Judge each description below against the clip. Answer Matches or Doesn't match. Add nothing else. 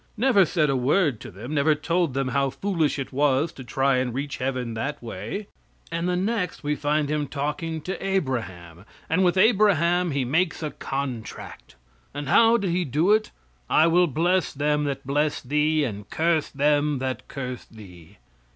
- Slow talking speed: Doesn't match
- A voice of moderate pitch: Matches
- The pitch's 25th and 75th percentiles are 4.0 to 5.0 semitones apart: Matches